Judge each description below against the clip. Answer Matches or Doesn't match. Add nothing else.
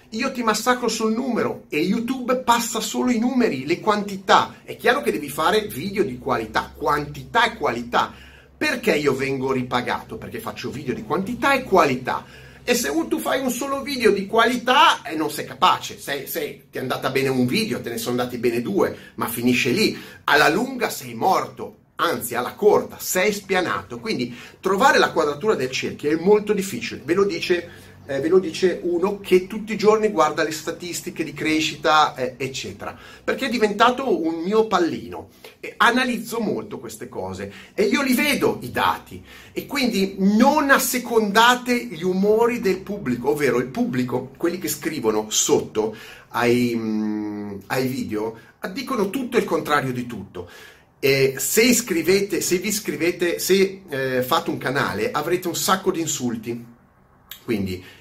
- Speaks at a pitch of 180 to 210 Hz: Matches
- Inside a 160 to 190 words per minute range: Matches